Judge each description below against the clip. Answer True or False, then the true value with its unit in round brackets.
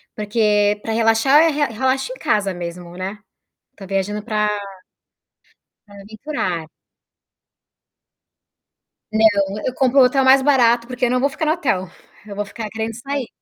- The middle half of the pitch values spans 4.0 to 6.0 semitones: True (4.3 semitones)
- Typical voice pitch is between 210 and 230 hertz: True (220 Hz)